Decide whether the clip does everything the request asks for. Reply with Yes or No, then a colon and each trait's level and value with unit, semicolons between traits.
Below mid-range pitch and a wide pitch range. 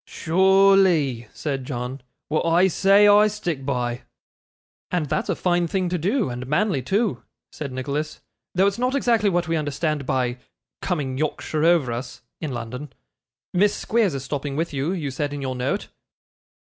No: medium, 155 Hz; wide, 6.1 semitones